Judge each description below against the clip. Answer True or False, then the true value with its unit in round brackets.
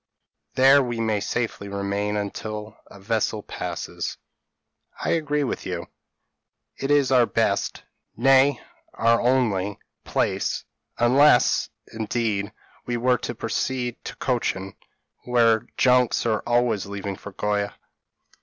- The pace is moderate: False (115 wpm)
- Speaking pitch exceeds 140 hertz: False (115 Hz)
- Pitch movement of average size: True (3.5 semitones)